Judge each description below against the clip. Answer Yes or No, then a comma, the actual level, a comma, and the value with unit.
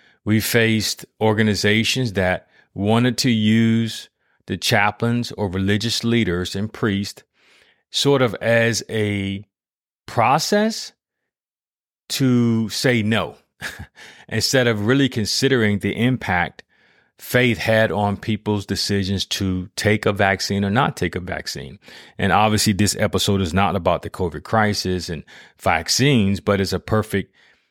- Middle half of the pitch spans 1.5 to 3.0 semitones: Yes, average, 2.7 semitones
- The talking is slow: Yes, slow, 125 wpm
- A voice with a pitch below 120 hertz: Yes, low, 105 Hz